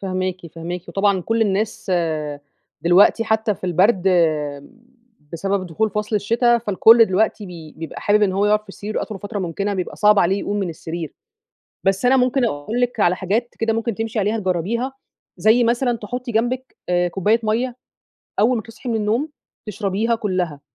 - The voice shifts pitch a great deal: No, average, 3.5 semitones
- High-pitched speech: Yes, high, 210 Hz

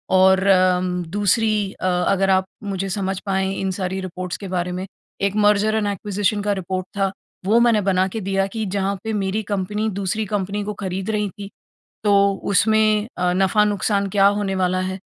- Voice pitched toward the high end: Yes, high, 195 Hz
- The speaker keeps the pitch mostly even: Yes, narrow, 1.8 semitones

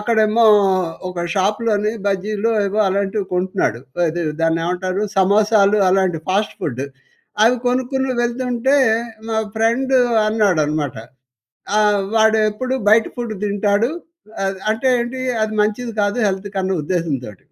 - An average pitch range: Yes, average, 3.1 semitones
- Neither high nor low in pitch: No, high, 210 Hz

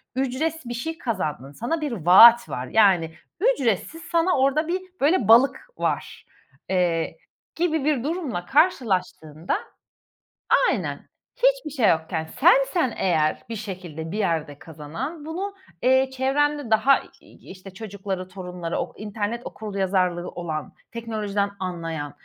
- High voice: Yes, high, 220 Hz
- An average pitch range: No, wide, 8.5 semitones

